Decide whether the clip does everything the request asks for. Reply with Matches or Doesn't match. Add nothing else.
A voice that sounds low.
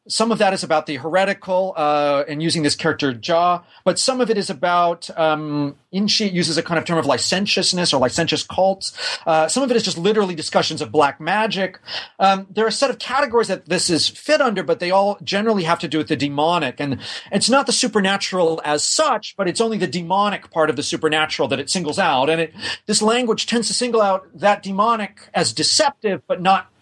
Doesn't match